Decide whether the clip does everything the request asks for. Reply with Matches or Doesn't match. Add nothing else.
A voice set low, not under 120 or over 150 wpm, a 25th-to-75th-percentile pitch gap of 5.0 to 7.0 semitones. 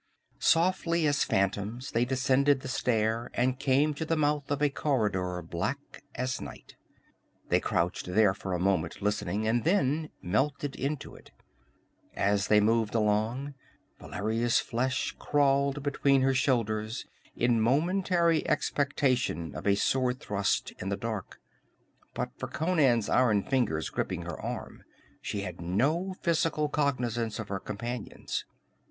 Matches